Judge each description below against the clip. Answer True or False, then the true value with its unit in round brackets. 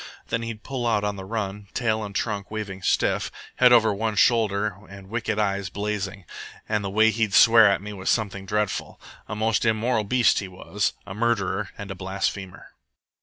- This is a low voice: True (105 Hz)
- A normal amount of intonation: False (2.2 semitones)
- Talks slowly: False (185 wpm)